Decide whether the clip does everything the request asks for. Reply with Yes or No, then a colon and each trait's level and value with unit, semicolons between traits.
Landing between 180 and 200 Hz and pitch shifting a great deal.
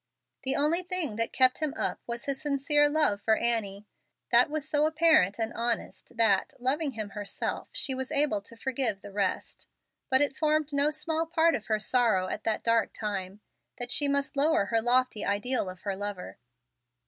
No: very high, 250 Hz; wide, 5.8 semitones